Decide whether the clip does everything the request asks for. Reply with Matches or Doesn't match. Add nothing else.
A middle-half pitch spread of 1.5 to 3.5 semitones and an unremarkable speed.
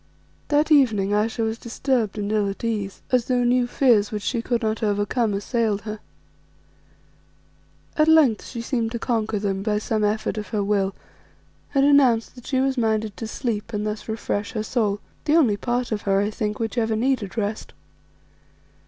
Matches